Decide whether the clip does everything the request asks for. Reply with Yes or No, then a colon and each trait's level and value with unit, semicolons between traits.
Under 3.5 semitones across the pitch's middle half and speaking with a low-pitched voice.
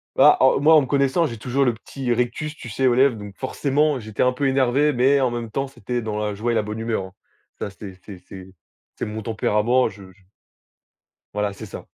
No: average, 4.2 semitones; low, 120 Hz